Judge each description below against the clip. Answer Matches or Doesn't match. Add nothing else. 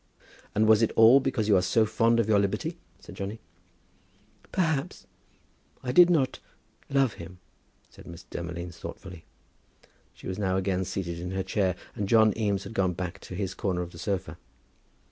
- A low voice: Matches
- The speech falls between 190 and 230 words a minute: Doesn't match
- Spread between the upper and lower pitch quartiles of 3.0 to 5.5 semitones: Matches